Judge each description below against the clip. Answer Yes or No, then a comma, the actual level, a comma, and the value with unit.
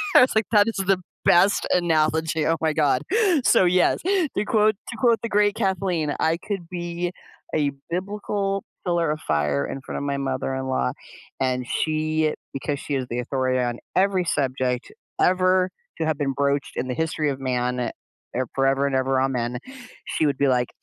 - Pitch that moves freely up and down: Yes, wide, 5.7 semitones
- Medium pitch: Yes, medium, 155 Hz